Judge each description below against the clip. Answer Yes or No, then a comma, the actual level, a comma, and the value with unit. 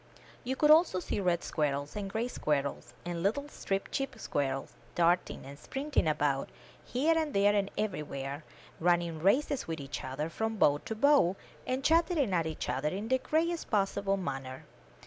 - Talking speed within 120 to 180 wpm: Yes, average, 170 wpm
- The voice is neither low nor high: No, high, 195 Hz